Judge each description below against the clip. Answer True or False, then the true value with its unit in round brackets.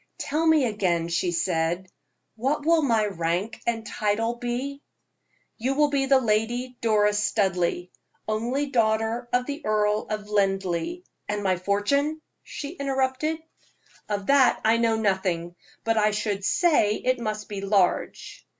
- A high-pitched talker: True (220 Hz)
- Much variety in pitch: False (4.6 semitones)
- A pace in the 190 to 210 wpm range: False (145 wpm)